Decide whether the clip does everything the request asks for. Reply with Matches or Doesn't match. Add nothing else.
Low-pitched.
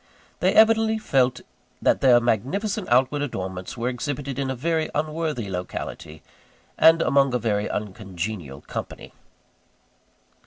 Matches